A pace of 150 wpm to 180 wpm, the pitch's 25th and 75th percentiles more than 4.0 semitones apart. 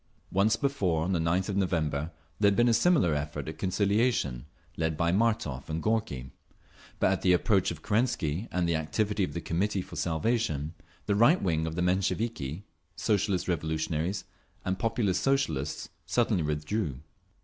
Yes: average, 160 wpm; average, 5.1 semitones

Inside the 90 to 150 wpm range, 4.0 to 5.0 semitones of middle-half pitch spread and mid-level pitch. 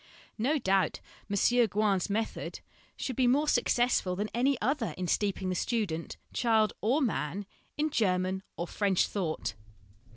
No: average, 140 wpm; average, 4.5 semitones; high, 210 Hz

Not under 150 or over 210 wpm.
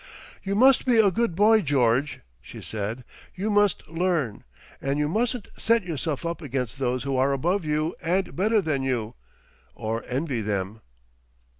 Yes: average, 160 wpm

